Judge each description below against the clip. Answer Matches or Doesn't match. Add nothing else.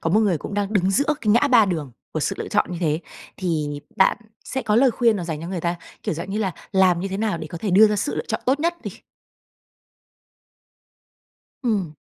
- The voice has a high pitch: Matches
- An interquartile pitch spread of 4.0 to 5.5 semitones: Matches